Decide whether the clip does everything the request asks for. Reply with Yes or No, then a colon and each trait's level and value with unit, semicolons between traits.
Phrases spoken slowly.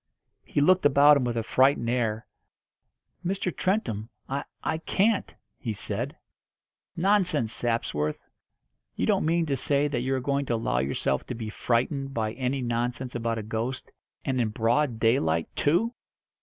No: average, 155 wpm